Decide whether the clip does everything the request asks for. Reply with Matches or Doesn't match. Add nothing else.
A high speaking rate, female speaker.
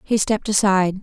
Doesn't match